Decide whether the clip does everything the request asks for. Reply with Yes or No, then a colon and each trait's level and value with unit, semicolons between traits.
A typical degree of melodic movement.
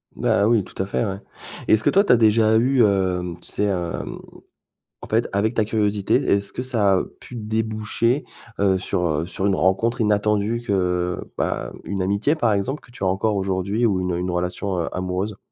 Yes: average, 3.0 semitones